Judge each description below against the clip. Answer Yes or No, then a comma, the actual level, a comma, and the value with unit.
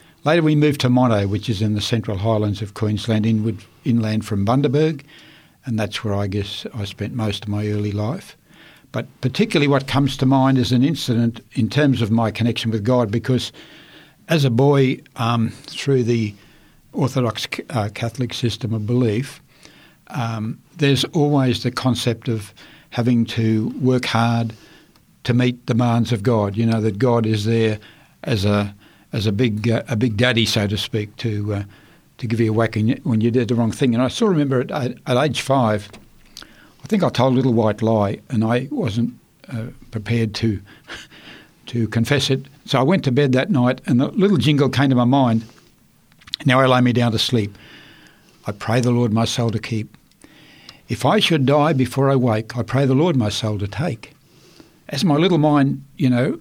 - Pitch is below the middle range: Yes, low, 120 Hz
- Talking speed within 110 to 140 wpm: No, average, 190 wpm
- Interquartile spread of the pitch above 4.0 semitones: No, average, 3.2 semitones